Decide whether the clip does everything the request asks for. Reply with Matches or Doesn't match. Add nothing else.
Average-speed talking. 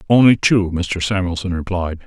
Matches